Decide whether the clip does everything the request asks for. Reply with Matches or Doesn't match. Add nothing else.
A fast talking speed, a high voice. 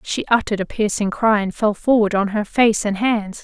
Matches